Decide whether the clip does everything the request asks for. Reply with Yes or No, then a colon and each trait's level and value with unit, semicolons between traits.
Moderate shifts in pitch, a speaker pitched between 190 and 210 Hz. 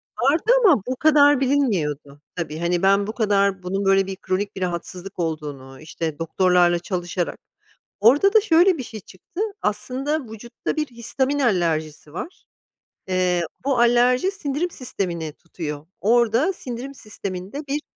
No: wide, 7.5 semitones; high, 200 Hz